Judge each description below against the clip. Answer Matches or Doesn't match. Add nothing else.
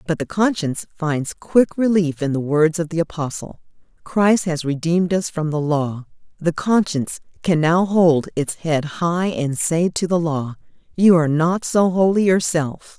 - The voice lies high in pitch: Doesn't match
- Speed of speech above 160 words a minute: Matches